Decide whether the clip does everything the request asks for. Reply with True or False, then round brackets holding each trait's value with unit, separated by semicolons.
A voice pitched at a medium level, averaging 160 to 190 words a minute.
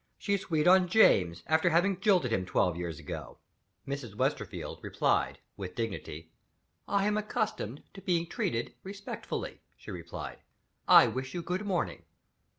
False (160 Hz; 145 wpm)